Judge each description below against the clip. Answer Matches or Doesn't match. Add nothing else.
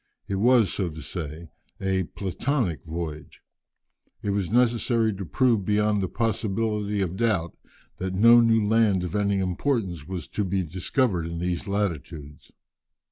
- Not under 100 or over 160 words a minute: Matches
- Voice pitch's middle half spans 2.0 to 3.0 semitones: Doesn't match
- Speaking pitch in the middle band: Doesn't match